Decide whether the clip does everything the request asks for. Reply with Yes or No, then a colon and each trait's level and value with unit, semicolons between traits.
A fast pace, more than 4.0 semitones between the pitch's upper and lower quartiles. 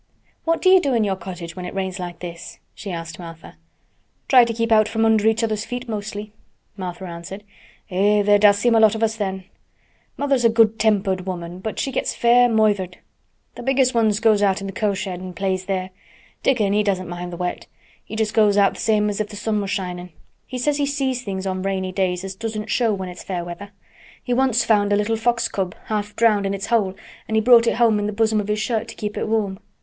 No: fast, 235 wpm; average, 2.9 semitones